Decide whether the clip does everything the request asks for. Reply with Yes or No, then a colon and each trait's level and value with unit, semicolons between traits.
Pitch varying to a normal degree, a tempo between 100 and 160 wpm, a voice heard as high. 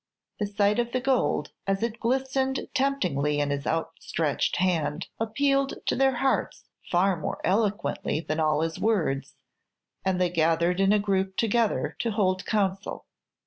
No: wide, 6.0 semitones; average, 150 wpm; high, 195 Hz